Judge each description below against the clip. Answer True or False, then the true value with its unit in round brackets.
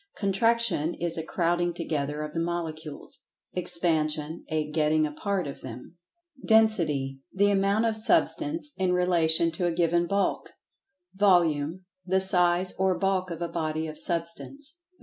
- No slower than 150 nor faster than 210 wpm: False (140 wpm)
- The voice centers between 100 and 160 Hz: False (175 Hz)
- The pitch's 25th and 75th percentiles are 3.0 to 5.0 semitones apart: True (3.4 semitones)